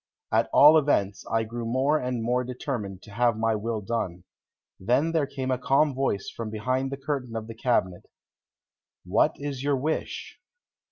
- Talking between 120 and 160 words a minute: No, average, 170 wpm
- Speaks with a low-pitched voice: Yes, low, 125 Hz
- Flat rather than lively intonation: No, average, 3.5 semitones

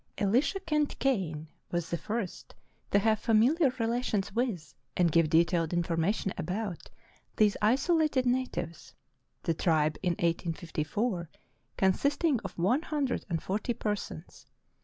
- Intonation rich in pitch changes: Yes, wide, 6.7 semitones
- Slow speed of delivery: Yes, slow, 125 wpm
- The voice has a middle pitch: No, high, 205 Hz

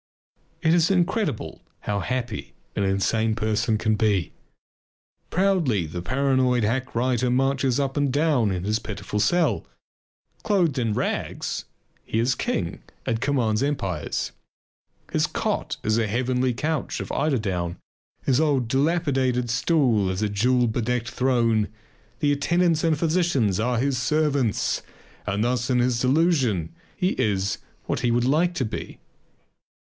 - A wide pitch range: No, average, 4.8 semitones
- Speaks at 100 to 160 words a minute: Yes, average, 140 wpm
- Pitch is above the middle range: No, low, 125 Hz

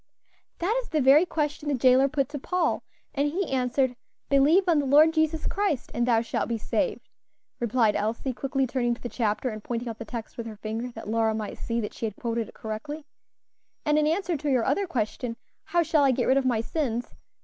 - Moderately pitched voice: No, very high, 260 Hz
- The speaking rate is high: Yes, fast, 220 wpm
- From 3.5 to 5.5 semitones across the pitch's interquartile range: Yes, average, 4.6 semitones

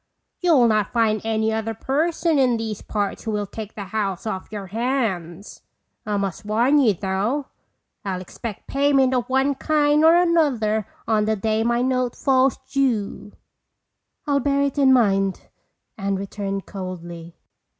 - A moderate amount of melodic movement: Yes, average, 5.0 semitones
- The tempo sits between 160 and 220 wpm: No, average, 150 wpm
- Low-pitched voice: No, high, 220 Hz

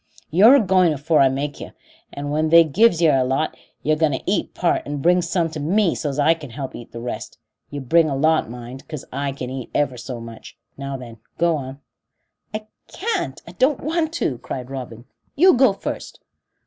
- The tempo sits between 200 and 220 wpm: Yes, fast, 205 wpm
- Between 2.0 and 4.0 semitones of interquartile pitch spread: No, average, 4.5 semitones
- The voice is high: No, medium, 150 Hz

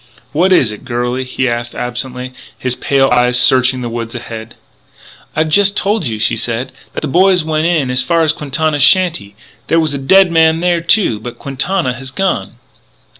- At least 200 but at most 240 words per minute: No, average, 185 wpm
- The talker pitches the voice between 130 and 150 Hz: Yes, low, 135 Hz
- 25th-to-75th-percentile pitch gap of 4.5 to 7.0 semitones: Yes, average, 5.2 semitones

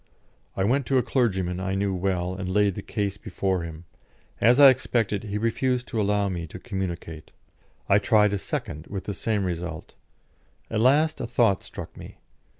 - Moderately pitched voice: No, low, 100 Hz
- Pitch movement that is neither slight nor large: Yes, average, 3.7 semitones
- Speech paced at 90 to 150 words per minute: No, average, 180 wpm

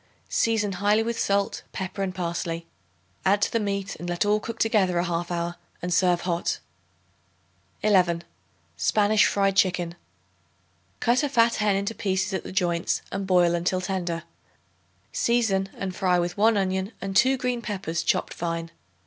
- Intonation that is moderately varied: Yes, average, 3.1 semitones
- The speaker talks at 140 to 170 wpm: Yes, average, 160 wpm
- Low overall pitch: No, high, 190 Hz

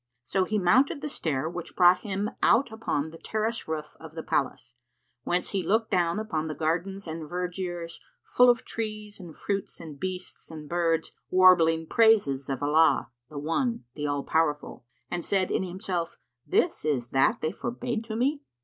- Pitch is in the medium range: Yes, medium, 175 Hz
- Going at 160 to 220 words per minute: Yes, average, 175 wpm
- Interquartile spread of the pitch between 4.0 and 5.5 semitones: Yes, average, 5.0 semitones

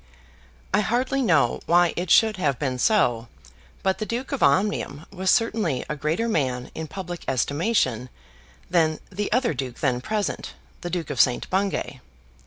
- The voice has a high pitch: No, medium, 175 Hz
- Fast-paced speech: No, average, 160 wpm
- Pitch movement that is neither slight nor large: No, wide, 7.2 semitones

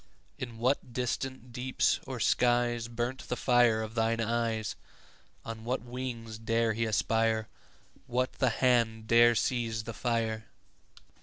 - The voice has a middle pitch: No, low, 115 Hz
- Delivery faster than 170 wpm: No, average, 140 wpm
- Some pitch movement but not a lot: No, narrow, 1.6 semitones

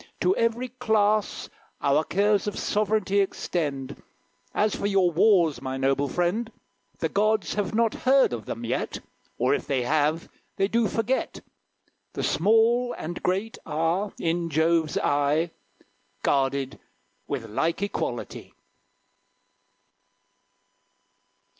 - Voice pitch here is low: No, medium, 180 Hz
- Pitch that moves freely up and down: Yes, wide, 6.7 semitones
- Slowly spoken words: Yes, slow, 115 wpm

